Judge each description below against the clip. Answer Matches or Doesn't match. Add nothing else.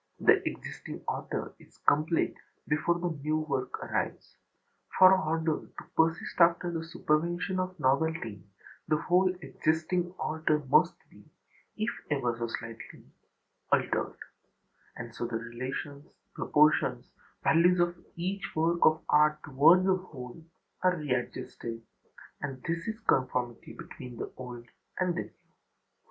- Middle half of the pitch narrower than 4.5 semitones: Doesn't match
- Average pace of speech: Doesn't match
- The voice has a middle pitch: Matches